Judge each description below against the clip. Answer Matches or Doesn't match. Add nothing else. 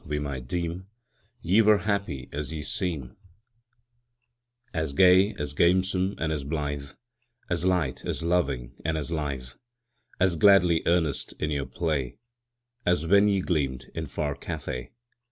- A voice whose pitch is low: Matches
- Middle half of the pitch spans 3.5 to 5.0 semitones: Matches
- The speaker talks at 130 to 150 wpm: Matches